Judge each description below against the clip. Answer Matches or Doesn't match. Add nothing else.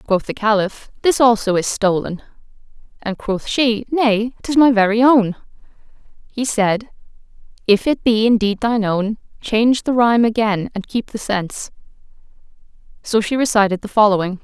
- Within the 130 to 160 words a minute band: Matches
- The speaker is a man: Doesn't match